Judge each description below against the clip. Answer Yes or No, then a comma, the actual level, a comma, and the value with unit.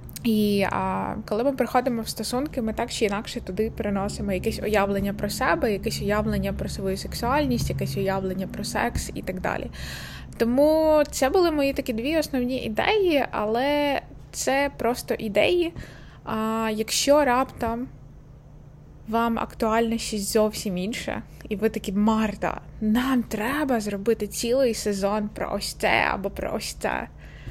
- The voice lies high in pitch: Yes, high, 220 Hz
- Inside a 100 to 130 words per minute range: No, average, 140 wpm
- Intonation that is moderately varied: Yes, average, 3.6 semitones